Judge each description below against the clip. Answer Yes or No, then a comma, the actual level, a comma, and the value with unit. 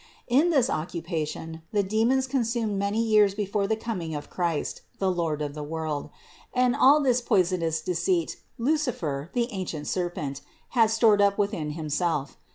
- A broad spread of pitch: Yes, wide, 6.0 semitones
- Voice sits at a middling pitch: No, high, 195 Hz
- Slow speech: No, average, 155 wpm